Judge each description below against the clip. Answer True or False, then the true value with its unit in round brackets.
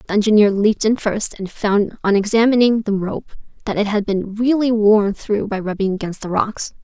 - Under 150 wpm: False (200 wpm)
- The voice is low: False (210 Hz)